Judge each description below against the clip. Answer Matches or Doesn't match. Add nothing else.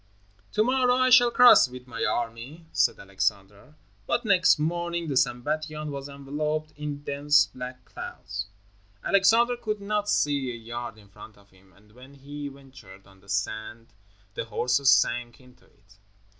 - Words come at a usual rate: Matches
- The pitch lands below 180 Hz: Matches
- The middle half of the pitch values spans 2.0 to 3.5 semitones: Doesn't match